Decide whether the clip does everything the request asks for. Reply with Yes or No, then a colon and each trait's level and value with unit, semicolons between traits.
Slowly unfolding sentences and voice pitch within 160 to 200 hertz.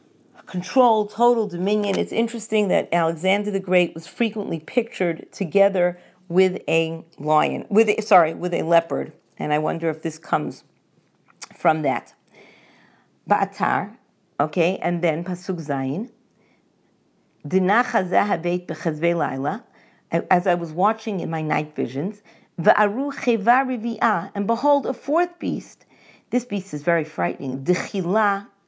Yes: slow, 115 wpm; medium, 185 Hz